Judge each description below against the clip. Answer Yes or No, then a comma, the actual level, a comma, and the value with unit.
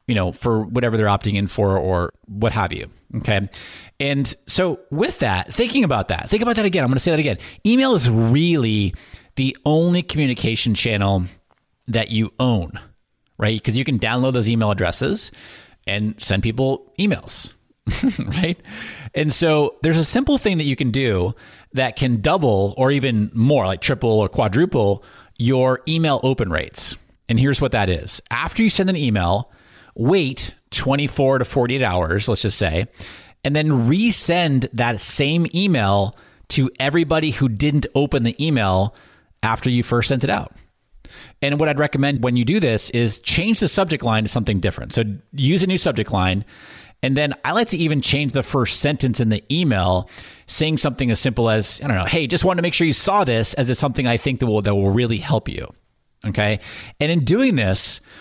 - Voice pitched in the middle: No, low, 125 Hz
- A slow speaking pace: No, average, 190 wpm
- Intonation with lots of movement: Yes, wide, 5.7 semitones